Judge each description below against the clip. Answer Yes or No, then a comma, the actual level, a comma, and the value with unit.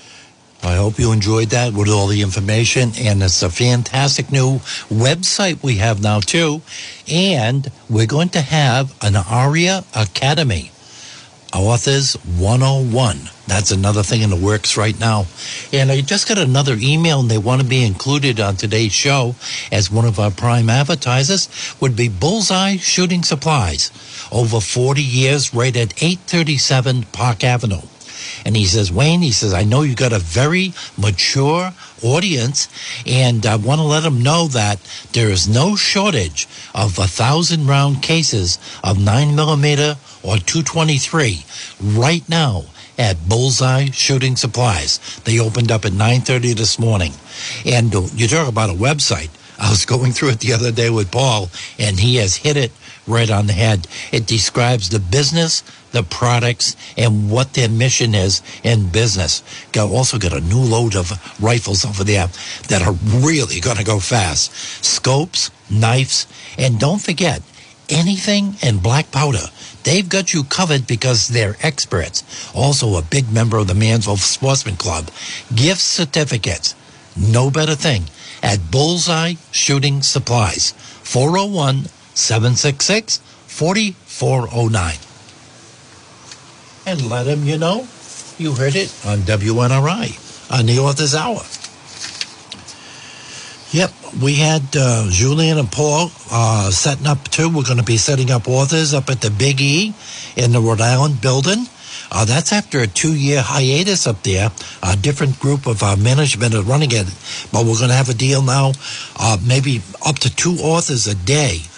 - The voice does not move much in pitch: No, average, 4.8 semitones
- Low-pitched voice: Yes, low, 125 Hz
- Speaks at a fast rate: No, average, 155 wpm